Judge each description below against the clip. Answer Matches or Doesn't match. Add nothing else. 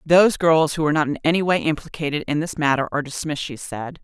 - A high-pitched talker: Doesn't match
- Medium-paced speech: Doesn't match